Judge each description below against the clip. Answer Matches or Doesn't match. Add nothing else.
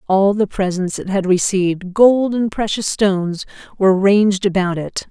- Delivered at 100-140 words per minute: Doesn't match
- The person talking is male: Doesn't match